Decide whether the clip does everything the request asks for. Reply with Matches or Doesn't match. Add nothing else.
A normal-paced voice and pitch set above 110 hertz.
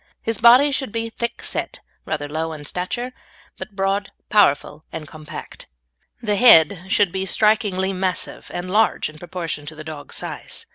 Matches